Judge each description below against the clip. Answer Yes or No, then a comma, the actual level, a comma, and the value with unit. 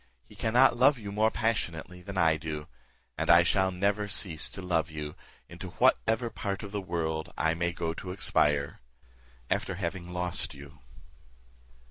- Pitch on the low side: Yes, very low, 90 Hz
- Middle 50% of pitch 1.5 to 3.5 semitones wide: No, average, 3.9 semitones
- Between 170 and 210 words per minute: No, average, 160 wpm